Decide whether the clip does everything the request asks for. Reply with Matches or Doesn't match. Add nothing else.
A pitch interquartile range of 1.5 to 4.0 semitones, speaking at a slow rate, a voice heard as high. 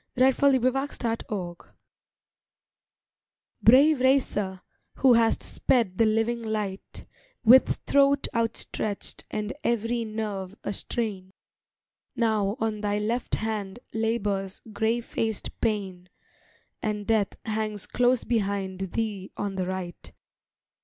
Matches